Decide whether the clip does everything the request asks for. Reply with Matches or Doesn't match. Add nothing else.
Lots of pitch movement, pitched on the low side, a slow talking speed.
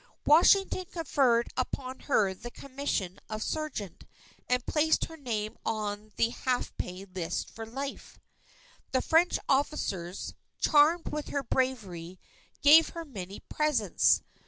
Doesn't match